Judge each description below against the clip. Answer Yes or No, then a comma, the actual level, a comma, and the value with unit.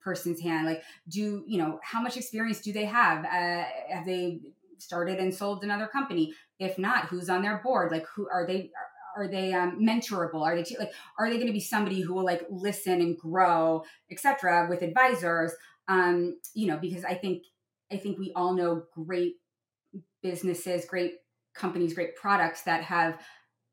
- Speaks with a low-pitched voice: No, medium, 180 Hz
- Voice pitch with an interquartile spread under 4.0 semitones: Yes, average, 2.9 semitones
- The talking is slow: No, average, 180 wpm